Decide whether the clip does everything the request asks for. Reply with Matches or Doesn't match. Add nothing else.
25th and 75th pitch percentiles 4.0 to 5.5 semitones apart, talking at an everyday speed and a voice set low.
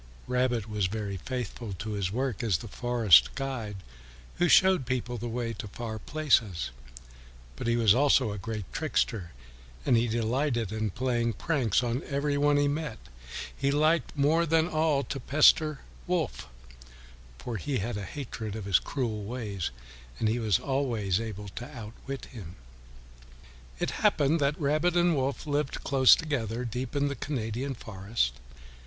Matches